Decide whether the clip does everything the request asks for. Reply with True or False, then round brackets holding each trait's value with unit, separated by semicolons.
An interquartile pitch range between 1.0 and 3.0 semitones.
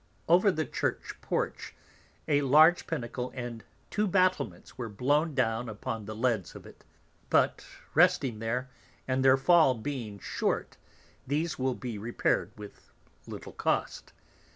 False (5.1 semitones)